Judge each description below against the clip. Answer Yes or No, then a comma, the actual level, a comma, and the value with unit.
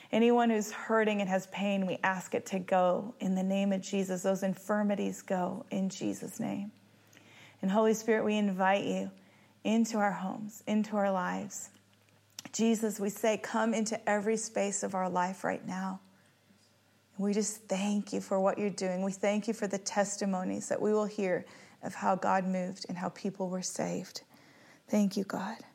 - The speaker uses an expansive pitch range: No, average, 2.7 semitones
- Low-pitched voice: No, high, 195 Hz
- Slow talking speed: No, average, 175 wpm